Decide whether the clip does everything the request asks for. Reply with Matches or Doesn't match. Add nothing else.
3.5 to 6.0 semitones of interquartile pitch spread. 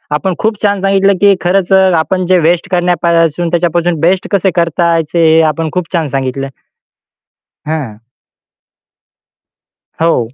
Doesn't match